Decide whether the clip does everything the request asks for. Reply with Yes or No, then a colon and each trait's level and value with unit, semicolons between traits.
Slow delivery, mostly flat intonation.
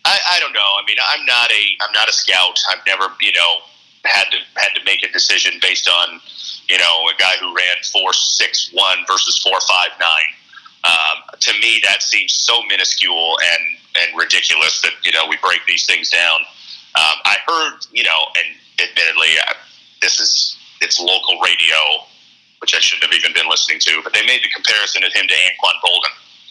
No: average, 200 wpm; narrow, 2.2 semitones